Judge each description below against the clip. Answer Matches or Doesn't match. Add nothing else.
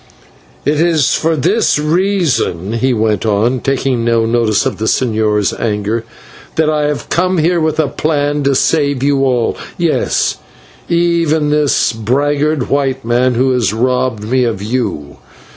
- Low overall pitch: Matches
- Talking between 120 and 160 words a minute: Matches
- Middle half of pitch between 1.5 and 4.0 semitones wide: Doesn't match